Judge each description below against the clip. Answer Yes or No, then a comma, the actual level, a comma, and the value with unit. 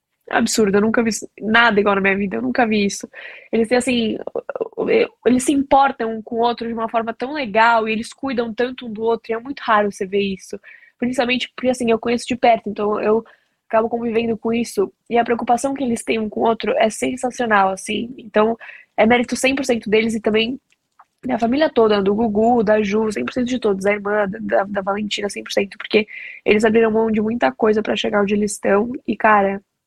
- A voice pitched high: Yes, high, 230 Hz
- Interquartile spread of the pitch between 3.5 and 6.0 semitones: No, narrow, 2.6 semitones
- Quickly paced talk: Yes, fast, 210 wpm